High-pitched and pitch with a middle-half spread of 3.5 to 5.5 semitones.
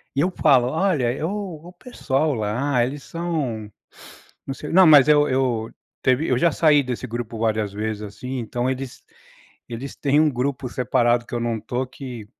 No: low, 130 Hz; average, 3.8 semitones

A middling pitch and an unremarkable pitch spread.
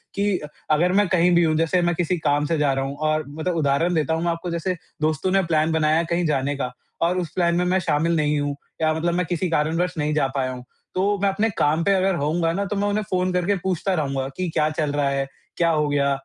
Yes: medium, 165 Hz; average, 3.3 semitones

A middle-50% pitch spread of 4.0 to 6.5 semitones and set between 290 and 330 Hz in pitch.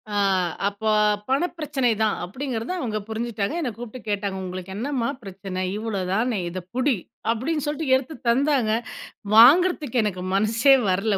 No: average, 5.0 semitones; high, 230 Hz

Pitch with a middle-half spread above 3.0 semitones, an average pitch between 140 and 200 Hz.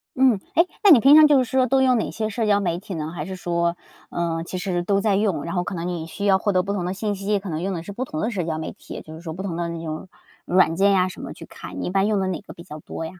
Yes: average, 3.5 semitones; medium, 185 Hz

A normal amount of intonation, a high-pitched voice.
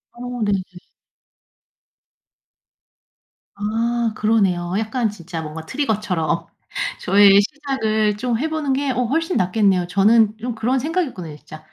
Yes: average, 4.6 semitones; high, 220 Hz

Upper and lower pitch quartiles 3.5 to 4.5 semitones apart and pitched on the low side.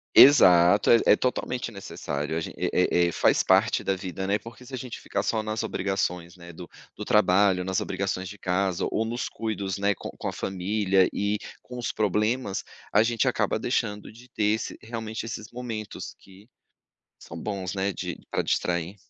No: average, 3.1 semitones; low, 100 Hz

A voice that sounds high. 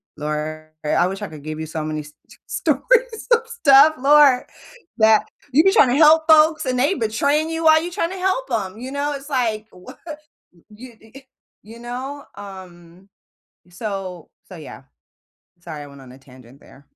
Yes: high, 230 Hz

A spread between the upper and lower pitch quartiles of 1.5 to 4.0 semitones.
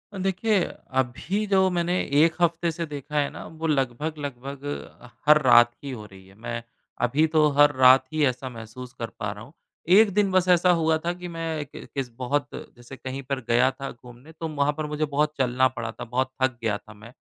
No: average, 4.7 semitones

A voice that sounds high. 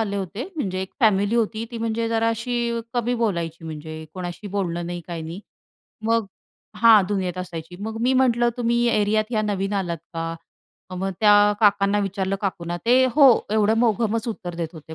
Yes: high, 205 Hz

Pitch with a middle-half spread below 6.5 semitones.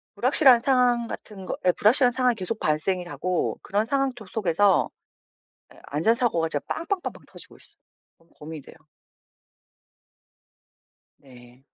No: wide, 6.8 semitones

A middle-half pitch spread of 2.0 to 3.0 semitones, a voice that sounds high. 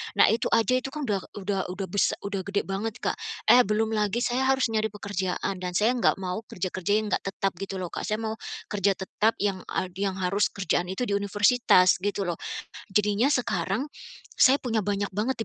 Yes: average, 2.7 semitones; high, 205 Hz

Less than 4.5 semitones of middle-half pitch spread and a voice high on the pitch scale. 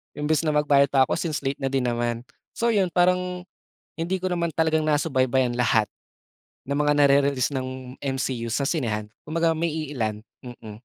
No: average, 3.9 semitones; medium, 140 Hz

